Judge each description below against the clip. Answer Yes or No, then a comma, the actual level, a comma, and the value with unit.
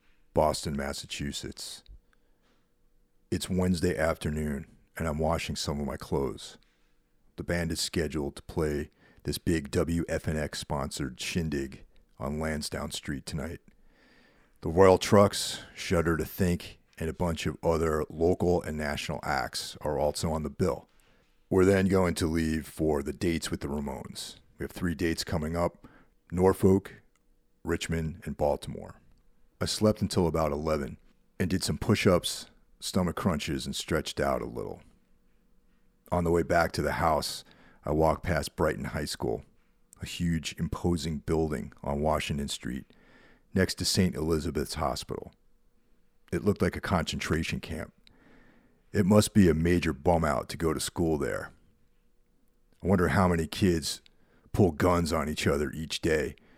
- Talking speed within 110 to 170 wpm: Yes, average, 150 wpm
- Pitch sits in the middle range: No, very low, 80 Hz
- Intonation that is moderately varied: Yes, average, 3.4 semitones